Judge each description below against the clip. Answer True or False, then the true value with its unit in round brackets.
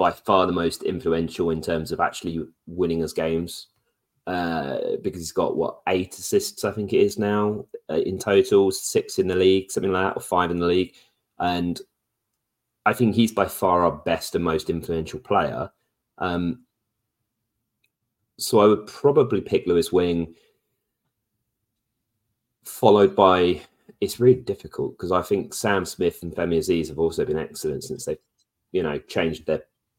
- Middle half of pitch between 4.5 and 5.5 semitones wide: True (5.2 semitones)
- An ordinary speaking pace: True (165 wpm)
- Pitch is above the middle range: False (105 Hz)